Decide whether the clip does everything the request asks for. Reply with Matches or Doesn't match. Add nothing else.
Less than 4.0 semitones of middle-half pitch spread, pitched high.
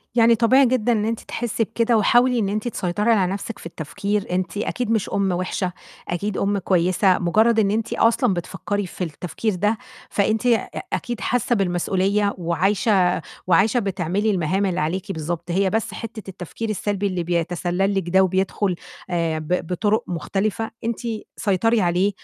Matches